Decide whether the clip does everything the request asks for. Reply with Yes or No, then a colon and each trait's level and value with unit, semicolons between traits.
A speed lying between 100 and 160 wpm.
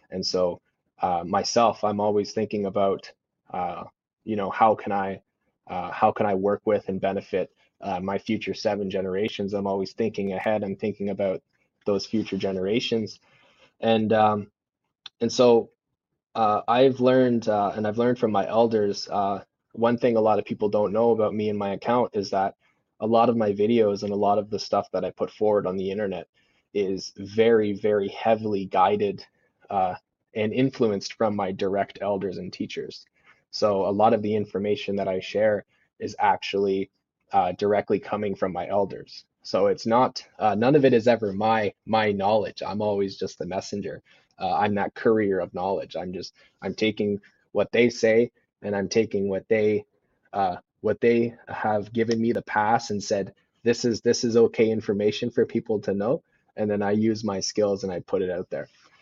No: average, 185 wpm